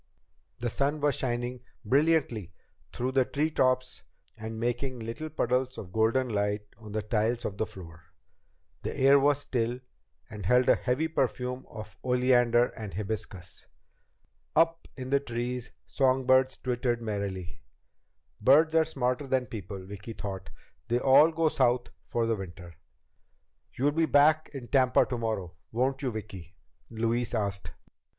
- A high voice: No, low, 120 Hz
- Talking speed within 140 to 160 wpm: Yes, average, 145 wpm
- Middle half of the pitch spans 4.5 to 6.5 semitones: No, average, 3.6 semitones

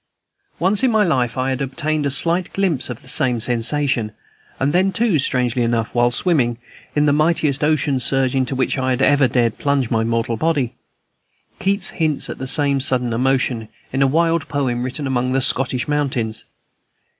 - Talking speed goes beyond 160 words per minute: Yes, average, 180 wpm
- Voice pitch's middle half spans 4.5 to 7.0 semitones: No, average, 3.5 semitones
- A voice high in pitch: No, low, 135 Hz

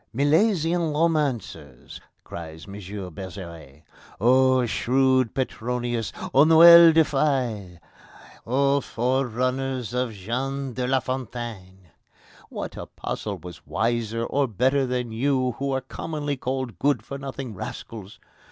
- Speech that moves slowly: Yes, slow, 115 wpm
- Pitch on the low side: Yes, low, 130 Hz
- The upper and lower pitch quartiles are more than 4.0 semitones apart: No, average, 3.4 semitones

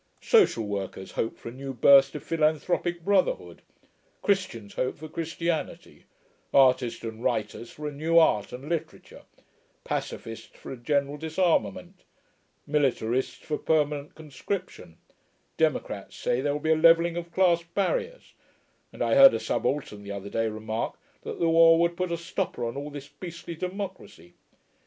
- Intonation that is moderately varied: No, wide, 5.8 semitones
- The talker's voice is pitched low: No, medium, 150 Hz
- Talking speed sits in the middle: Yes, average, 150 wpm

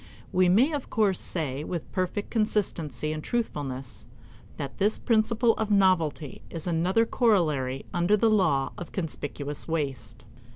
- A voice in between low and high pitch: Yes, medium, 175 Hz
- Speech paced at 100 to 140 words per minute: Yes, slow, 135 wpm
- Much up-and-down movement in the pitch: Yes, wide, 6.3 semitones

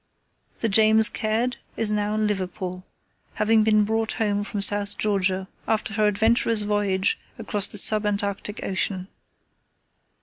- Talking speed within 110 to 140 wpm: Yes, slow, 135 wpm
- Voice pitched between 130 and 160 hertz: No, high, 210 Hz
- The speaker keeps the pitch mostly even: Yes, narrow, 1.5 semitones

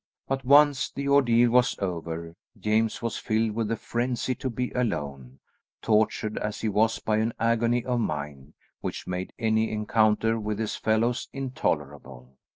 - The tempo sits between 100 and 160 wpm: Yes, average, 155 wpm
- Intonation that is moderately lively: Yes, average, 3.6 semitones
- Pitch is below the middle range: Yes, low, 110 Hz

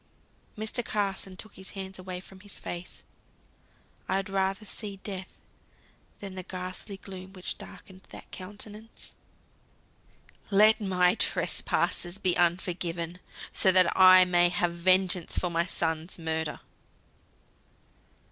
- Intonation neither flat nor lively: No, narrow, 1.6 semitones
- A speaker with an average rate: No, slow, 120 wpm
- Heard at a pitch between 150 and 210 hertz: Yes, medium, 185 Hz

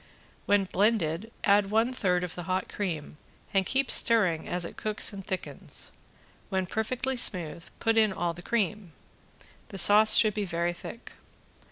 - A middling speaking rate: Yes, average, 160 wpm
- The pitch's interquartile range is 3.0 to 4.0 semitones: Yes, average, 3.7 semitones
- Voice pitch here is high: Yes, high, 195 Hz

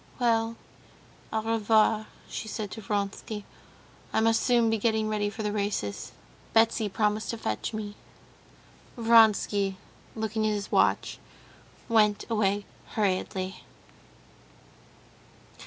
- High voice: Yes, high, 215 Hz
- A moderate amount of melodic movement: No, narrow, 1.5 semitones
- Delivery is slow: Yes, slow, 110 wpm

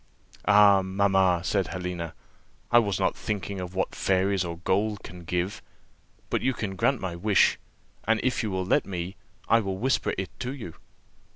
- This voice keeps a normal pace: Yes, average, 175 wpm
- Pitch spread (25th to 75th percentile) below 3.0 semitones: Yes, narrow, 2.4 semitones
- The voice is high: No, very low, 95 Hz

